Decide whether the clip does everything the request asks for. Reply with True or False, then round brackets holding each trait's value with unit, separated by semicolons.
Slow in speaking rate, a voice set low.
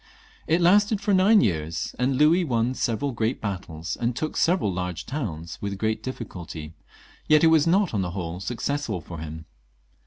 False (175 wpm; 115 Hz)